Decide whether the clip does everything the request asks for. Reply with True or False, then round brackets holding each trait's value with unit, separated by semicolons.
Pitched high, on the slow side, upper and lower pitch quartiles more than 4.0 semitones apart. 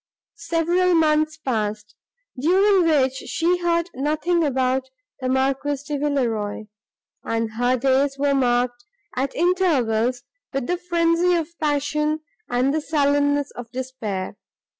True (285 Hz; 120 wpm; 4.6 semitones)